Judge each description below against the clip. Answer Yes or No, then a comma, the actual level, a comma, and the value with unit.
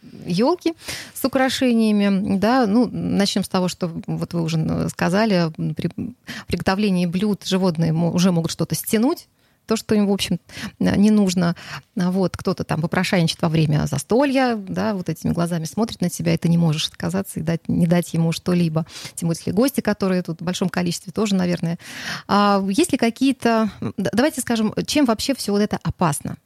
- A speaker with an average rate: No, fast, 170 wpm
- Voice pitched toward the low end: No, high, 190 Hz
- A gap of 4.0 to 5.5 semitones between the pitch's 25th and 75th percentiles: Yes, average, 4.4 semitones